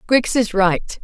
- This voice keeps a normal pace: Yes, average, 175 wpm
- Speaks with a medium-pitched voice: No, high, 215 Hz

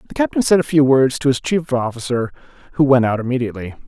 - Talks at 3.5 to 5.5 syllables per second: No, 6.6 syllables/s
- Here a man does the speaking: Yes, male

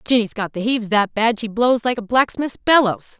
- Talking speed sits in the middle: No, fast, 225 wpm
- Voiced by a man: No, female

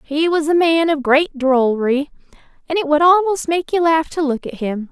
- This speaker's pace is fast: Yes, fast, 220 wpm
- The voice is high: Yes, very high, 300 Hz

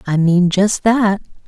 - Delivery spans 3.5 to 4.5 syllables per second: Yes, 3.6 syllables/s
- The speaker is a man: No, female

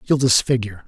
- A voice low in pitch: Yes, low, 120 Hz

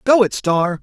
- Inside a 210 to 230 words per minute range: Yes, fast, 215 wpm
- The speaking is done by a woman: No, male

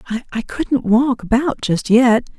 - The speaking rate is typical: Yes, average, 150 wpm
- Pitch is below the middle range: No, high, 240 Hz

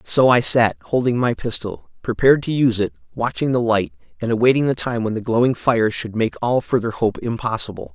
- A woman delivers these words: No, male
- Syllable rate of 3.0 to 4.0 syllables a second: No, 5.7 syllables/s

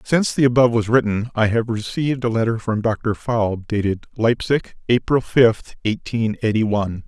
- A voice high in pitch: No, low, 115 Hz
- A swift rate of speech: No, average, 170 wpm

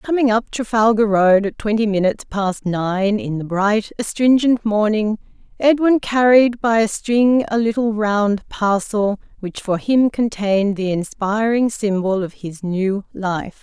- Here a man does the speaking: No, female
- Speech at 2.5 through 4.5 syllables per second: Yes, 4.1 syllables/s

